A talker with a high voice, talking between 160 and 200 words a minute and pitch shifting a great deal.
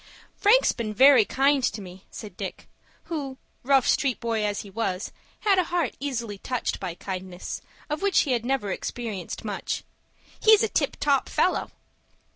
Yes: high, 240 Hz; average, 165 wpm; wide, 5.7 semitones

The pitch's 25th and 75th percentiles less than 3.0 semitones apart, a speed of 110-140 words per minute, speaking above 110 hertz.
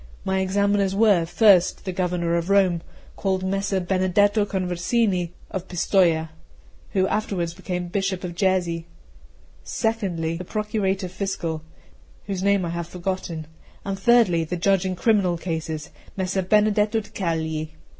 Yes: narrow, 2.6 semitones; slow, 135 wpm; medium, 185 Hz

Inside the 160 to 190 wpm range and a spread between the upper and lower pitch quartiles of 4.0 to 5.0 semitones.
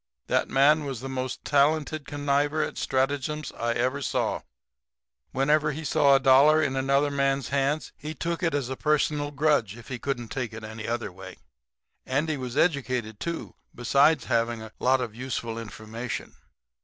No: average, 165 wpm; average, 3.4 semitones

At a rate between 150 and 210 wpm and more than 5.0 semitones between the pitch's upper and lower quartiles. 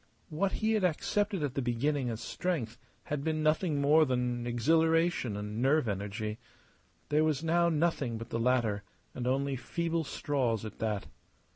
Yes: average, 160 wpm; wide, 5.5 semitones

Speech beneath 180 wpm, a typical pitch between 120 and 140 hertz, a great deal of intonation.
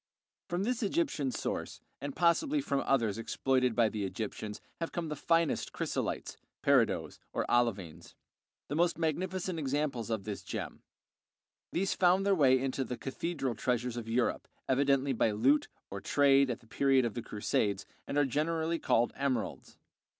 Yes: average, 155 wpm; low, 135 Hz; wide, 5.9 semitones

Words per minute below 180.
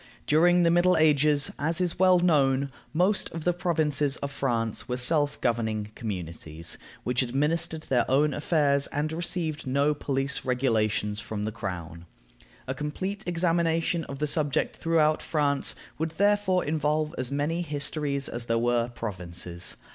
Yes: average, 145 wpm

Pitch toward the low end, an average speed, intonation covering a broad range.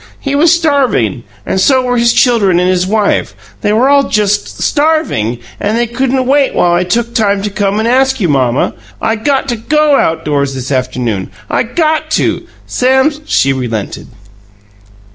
No: high, 225 Hz; average, 175 wpm; wide, 7.6 semitones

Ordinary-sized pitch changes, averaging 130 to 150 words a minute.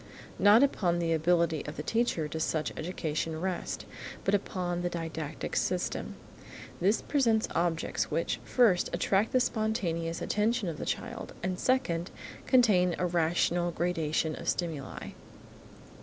Yes: average, 3.9 semitones; slow, 135 wpm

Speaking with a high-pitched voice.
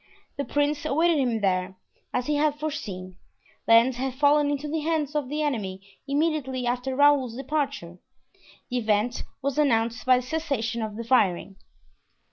Yes: very high, 260 Hz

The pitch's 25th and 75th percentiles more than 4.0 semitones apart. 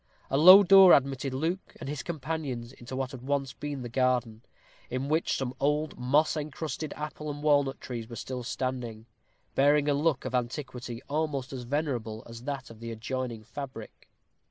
No: average, 3.2 semitones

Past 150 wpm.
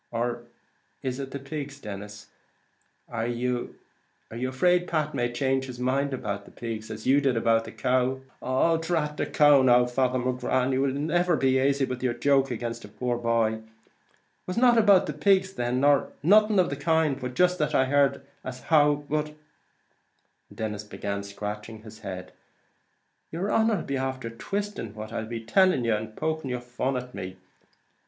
Yes: average, 185 wpm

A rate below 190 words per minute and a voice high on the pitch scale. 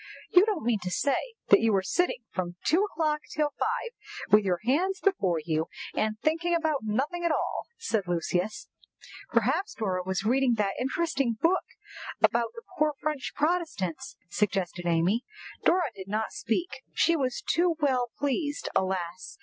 Yes: average, 160 wpm; very high, 250 Hz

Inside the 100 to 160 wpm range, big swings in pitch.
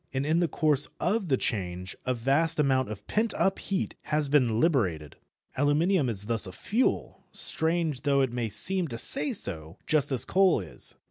No: average, 185 wpm; wide, 6.5 semitones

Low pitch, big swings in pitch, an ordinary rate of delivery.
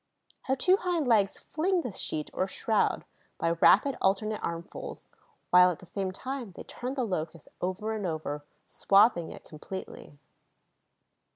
No: high, 195 Hz; wide, 6.3 semitones; average, 150 wpm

